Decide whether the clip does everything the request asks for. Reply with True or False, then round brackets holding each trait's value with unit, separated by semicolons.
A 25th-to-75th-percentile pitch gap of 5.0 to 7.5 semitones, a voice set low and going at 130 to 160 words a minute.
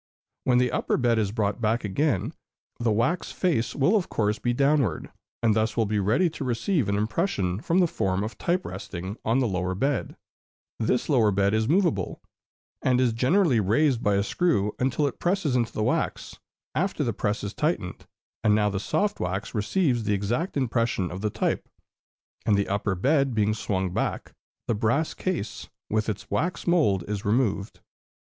False (5.6 semitones; 115 Hz; 180 wpm)